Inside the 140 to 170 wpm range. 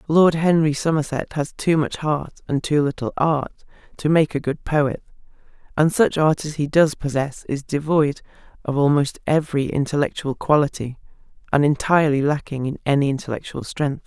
Yes: average, 160 wpm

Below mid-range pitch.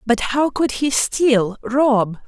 No: very high, 250 Hz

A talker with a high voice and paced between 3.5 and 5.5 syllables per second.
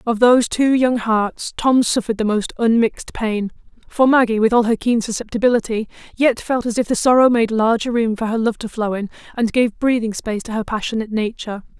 No: high, 230 Hz; 5.8 syllables/s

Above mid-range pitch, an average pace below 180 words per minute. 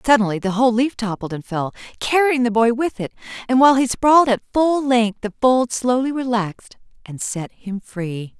No: high, 235 Hz; average, 195 wpm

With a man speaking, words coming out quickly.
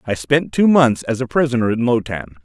Yes: male; fast, 245 wpm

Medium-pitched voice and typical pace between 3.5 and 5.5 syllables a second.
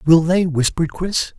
Yes: medium, 165 Hz; 4.9 syllables/s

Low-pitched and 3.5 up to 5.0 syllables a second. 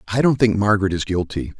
No: low, 100 Hz; 6.4 syllables/s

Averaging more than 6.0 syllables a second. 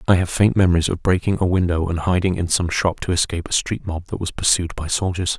Yes: 6.2 syllables/s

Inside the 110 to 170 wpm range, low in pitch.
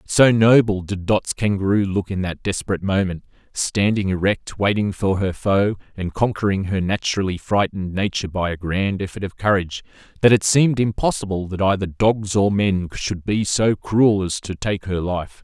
No: average, 180 wpm; low, 100 Hz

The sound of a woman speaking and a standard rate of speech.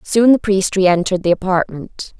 Yes: female; average, 165 wpm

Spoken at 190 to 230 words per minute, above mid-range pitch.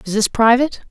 Yes: average, 200 wpm; high, 235 Hz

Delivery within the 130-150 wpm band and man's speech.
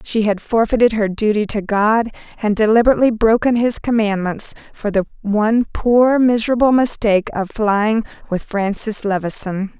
No: average, 140 wpm; female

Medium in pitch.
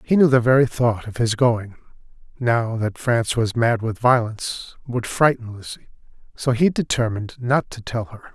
No: low, 120 Hz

